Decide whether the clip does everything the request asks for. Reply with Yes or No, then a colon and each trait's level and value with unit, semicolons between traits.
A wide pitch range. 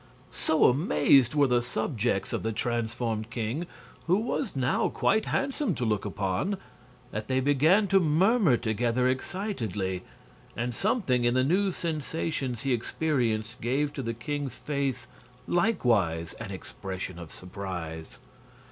Yes: wide, 5.9 semitones